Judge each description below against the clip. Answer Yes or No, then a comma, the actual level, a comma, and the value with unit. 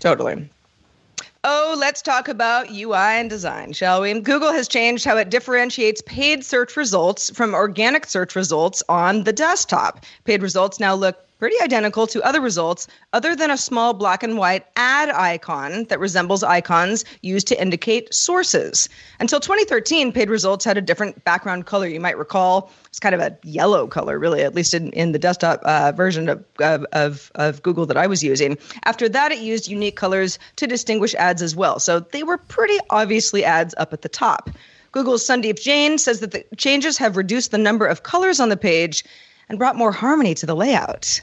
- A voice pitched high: Yes, high, 215 Hz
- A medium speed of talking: Yes, average, 190 wpm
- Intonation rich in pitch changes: Yes, wide, 5.7 semitones